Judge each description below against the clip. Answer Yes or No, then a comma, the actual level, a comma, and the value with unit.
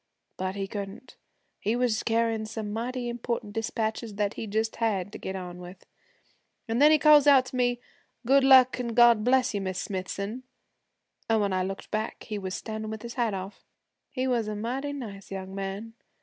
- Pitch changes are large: No, average, 3.6 semitones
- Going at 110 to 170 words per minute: No, average, 190 wpm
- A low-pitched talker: No, high, 220 Hz